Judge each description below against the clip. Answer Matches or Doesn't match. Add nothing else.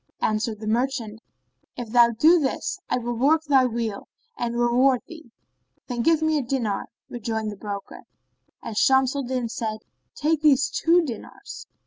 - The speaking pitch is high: Matches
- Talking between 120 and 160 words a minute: Matches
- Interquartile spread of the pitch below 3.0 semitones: Doesn't match